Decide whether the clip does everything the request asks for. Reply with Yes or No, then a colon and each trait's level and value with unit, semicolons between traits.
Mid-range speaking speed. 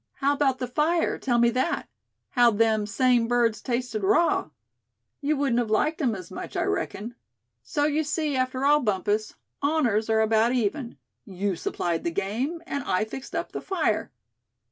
Yes: average, 170 wpm